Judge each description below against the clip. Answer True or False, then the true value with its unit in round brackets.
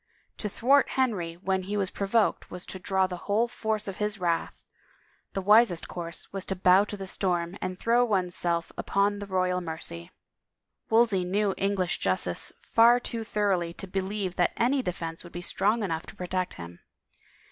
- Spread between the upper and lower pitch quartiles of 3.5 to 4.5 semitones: False (2.9 semitones)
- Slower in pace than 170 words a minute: False (180 wpm)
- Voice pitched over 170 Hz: True (190 Hz)